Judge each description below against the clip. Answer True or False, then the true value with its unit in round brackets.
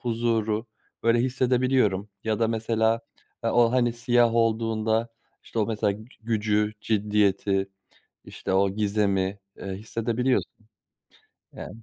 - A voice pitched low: True (110 Hz)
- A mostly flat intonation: True (2.0 semitones)